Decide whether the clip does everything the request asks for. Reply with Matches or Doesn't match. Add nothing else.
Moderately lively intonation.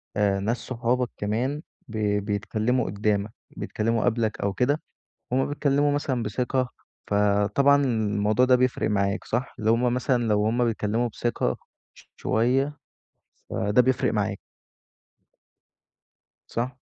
Matches